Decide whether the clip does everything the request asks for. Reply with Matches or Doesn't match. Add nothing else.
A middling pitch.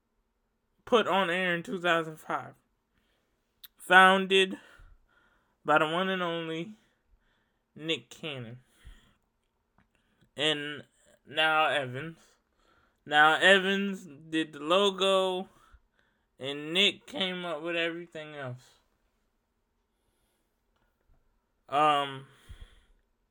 Matches